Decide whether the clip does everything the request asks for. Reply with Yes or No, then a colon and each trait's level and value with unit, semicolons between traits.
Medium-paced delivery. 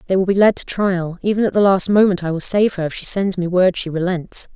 No: fast, 275 wpm